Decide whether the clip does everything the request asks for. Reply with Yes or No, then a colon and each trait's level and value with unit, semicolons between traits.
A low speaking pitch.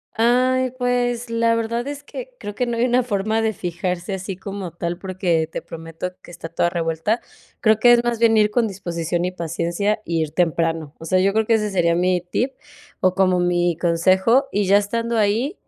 No: high, 195 Hz